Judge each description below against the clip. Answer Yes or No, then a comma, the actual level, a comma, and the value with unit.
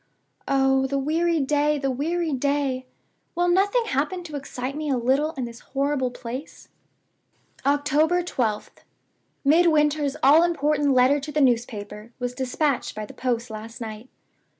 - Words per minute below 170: Yes, average, 145 wpm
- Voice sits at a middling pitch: No, very high, 275 Hz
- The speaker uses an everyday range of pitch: Yes, average, 3.3 semitones